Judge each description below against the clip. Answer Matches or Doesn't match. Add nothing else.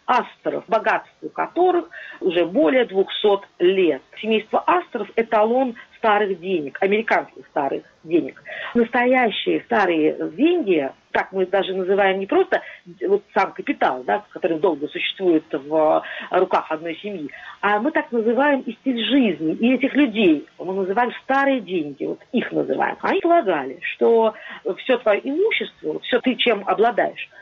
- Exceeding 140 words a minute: Doesn't match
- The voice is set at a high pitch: Matches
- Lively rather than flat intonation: Matches